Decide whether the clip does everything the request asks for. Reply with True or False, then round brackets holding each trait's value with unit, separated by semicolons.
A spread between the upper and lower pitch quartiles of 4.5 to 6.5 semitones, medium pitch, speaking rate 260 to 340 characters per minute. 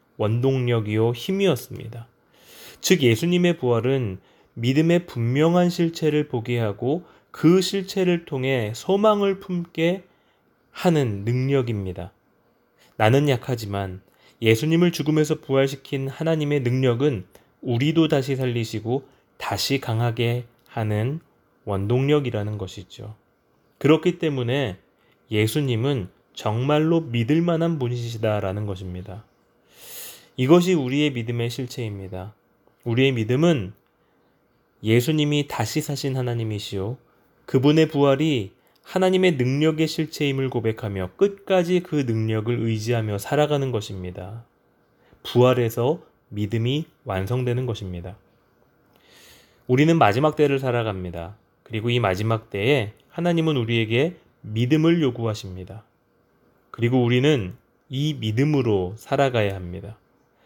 False (5.3 semitones; 125 Hz; 270 characters per minute)